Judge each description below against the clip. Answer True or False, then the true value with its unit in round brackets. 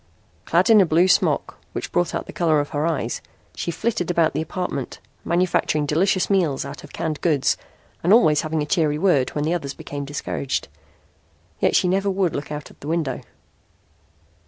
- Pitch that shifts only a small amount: False (3.5 semitones)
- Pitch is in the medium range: True (160 Hz)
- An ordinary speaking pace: True (180 wpm)